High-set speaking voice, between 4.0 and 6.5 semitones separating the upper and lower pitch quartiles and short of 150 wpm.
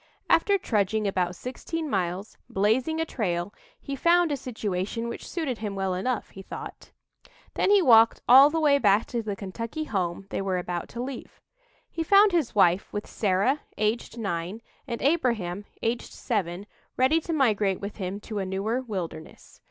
No: high, 220 Hz; wide, 5.5 semitones; average, 170 wpm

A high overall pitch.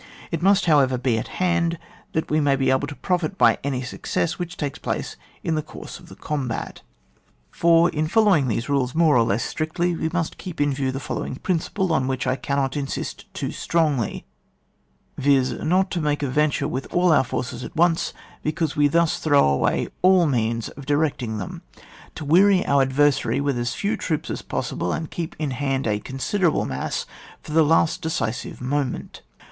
No: medium, 145 Hz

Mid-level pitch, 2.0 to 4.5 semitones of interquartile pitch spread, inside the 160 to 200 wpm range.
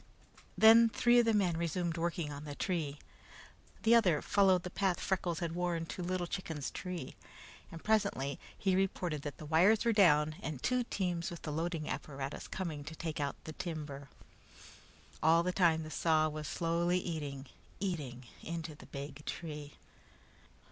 Yes: medium, 165 Hz; average, 3.3 semitones; average, 165 wpm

